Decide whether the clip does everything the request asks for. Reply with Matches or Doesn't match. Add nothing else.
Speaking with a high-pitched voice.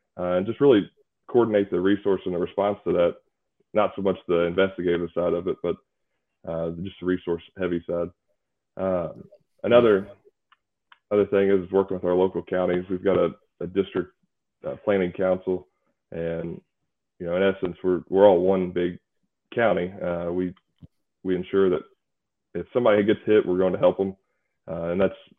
Doesn't match